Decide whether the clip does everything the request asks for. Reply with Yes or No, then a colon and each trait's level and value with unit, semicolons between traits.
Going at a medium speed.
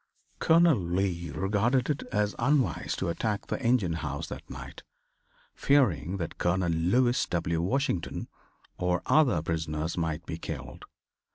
No: slow, 130 wpm